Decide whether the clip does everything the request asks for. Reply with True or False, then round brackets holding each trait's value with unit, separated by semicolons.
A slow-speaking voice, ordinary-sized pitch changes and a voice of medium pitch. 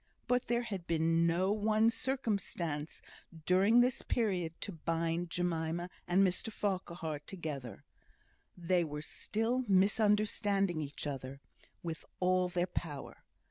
True (120 wpm; 4.1 semitones; 180 Hz)